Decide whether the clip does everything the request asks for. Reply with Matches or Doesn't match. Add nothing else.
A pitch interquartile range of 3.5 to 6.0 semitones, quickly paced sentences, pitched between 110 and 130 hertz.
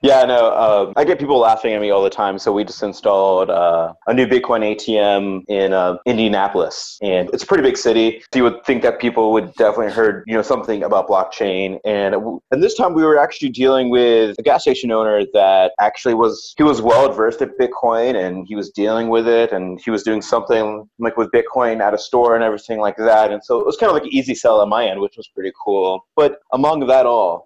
Matches